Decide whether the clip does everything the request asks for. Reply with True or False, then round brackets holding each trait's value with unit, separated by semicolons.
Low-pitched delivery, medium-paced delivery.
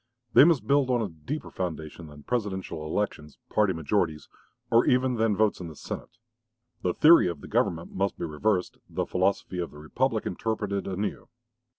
True (95 Hz; 175 wpm)